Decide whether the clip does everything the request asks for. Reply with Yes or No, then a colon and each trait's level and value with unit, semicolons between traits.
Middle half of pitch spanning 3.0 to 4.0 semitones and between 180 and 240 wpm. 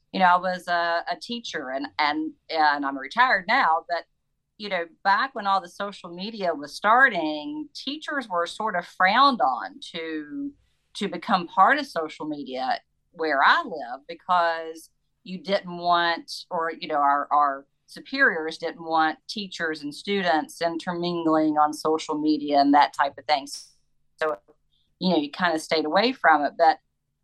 No: average, 3.7 semitones; average, 165 wpm